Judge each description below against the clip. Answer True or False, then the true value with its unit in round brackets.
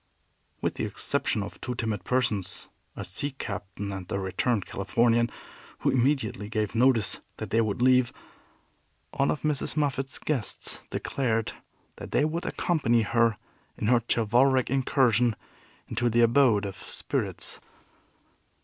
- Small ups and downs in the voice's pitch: False (3.6 semitones)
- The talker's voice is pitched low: True (120 Hz)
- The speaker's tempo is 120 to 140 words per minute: True (135 wpm)